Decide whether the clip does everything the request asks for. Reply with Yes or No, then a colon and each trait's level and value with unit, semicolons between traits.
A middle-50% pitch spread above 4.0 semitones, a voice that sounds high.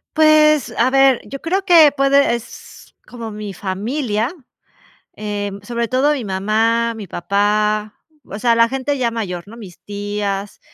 Yes: average, 4.6 semitones; high, 230 Hz